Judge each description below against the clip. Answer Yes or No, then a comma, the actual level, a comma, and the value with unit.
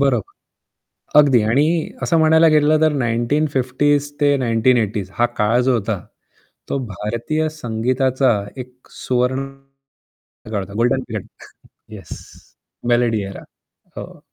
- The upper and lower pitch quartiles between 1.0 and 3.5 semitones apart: No, average, 4.0 semitones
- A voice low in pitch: Yes, low, 125 Hz